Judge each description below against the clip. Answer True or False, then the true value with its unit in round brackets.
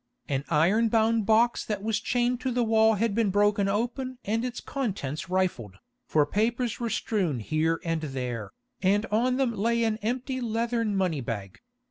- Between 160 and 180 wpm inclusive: True (170 wpm)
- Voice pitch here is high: True (215 Hz)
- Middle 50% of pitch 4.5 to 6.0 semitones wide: True (5.4 semitones)